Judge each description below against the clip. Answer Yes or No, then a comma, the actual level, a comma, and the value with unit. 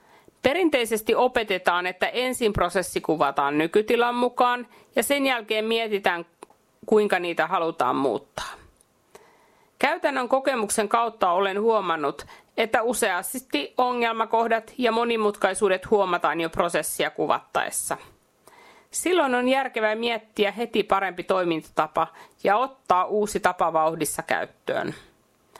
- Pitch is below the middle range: No, high, 215 Hz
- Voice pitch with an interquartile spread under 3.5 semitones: No, average, 4.8 semitones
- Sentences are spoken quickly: No, average, 100 wpm